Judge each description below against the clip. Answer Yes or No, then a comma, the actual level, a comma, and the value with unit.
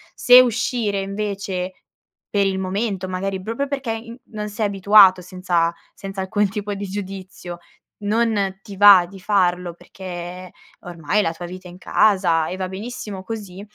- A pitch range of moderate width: No, narrow, 2.3 semitones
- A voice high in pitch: Yes, high, 195 Hz